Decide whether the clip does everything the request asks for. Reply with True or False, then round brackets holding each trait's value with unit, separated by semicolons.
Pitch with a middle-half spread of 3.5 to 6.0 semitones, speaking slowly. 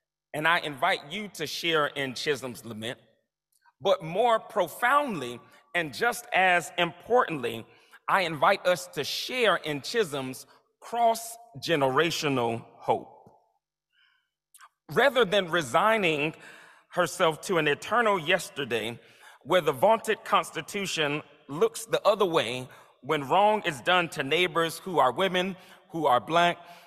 True (4.9 semitones; 120 wpm)